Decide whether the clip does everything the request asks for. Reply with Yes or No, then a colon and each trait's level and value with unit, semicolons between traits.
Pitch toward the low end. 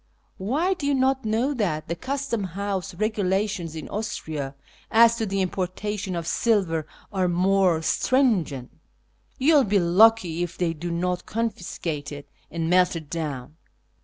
No: high, 190 Hz